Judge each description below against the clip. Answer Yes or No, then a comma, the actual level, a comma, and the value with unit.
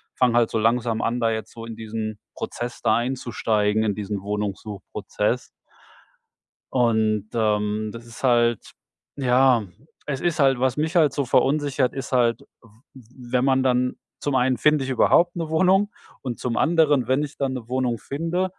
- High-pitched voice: No, low, 125 Hz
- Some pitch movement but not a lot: Yes, average, 3.5 semitones